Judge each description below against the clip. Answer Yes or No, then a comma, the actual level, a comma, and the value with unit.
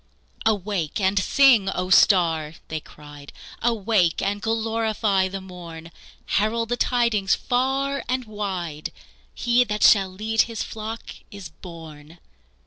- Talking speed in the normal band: No, slow, 125 wpm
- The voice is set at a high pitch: Yes, high, 200 Hz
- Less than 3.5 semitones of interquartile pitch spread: No, average, 4.5 semitones